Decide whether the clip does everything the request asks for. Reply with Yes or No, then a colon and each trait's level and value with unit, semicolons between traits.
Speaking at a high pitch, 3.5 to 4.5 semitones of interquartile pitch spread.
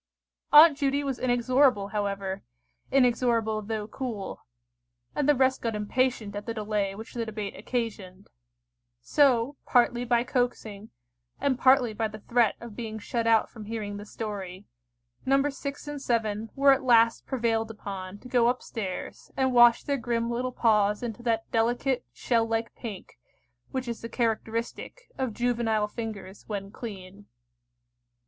No: high, 230 Hz; average, 3.1 semitones